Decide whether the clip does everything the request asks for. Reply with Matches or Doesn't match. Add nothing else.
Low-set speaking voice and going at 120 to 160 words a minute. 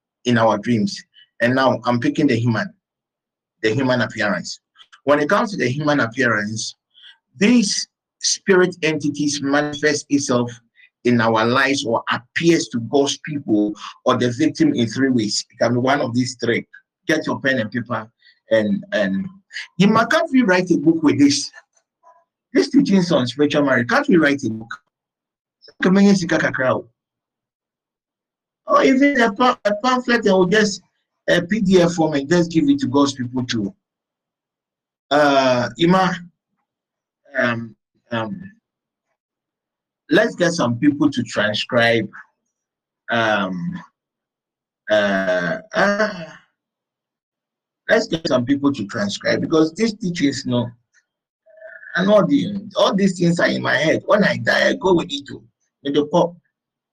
Doesn't match